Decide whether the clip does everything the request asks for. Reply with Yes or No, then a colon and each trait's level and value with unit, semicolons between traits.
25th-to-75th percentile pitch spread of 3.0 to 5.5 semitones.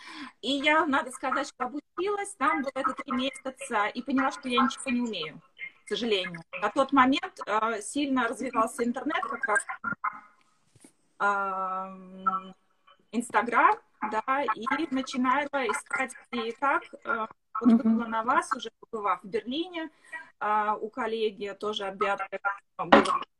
Yes: average, 4.5 semitones